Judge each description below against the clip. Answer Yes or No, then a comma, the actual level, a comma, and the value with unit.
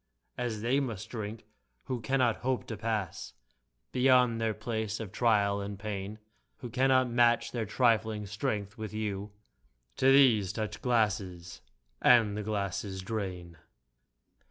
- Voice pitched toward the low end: Yes, low, 110 Hz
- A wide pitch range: No, average, 2.8 semitones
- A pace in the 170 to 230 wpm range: No, average, 140 wpm